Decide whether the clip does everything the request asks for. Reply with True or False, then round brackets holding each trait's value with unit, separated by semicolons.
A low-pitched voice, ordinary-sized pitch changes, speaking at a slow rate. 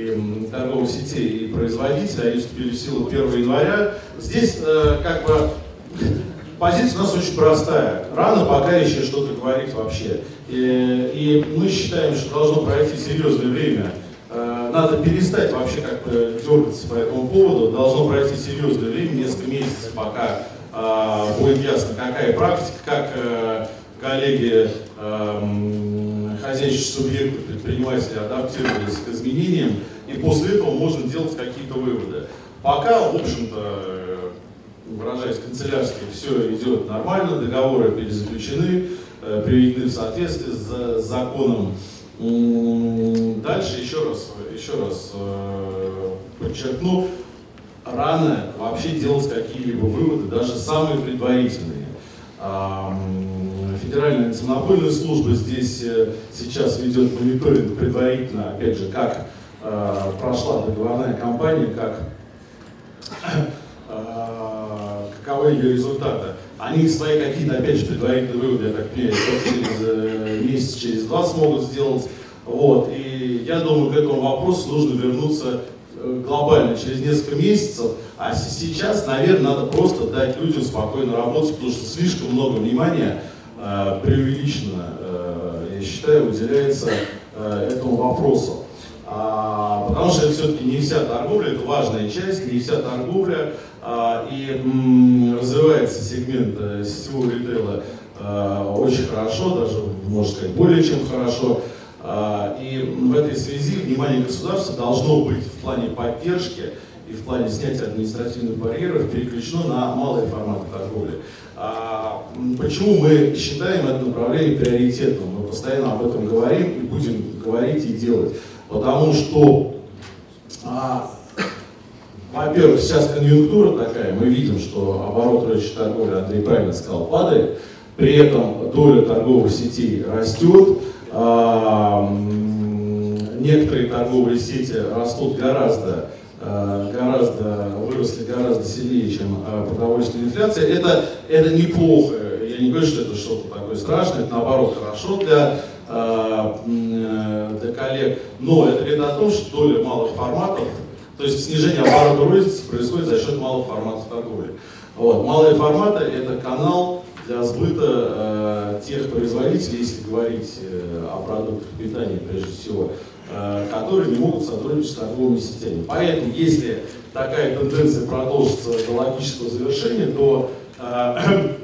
False (125 Hz; 4.6 semitones; 120 wpm)